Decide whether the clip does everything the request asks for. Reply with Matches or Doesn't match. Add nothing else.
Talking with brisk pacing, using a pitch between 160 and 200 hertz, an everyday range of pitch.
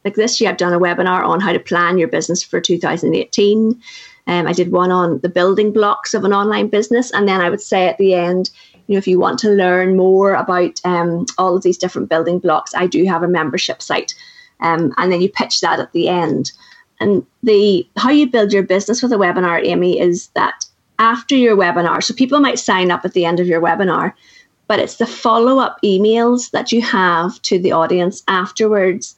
Matches